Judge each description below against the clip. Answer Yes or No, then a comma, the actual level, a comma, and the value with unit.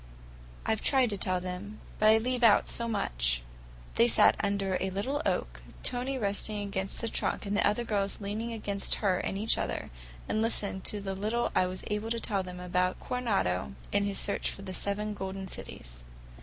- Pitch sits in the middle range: No, high, 200 Hz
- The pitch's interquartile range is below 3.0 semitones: Yes, narrow, 2.6 semitones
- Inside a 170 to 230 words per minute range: Yes, average, 195 wpm